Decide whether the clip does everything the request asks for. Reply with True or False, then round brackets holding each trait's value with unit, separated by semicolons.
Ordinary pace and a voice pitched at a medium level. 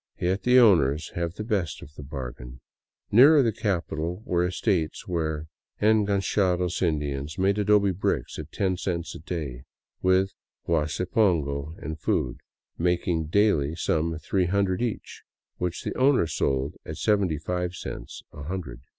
False (150 wpm; 90 Hz)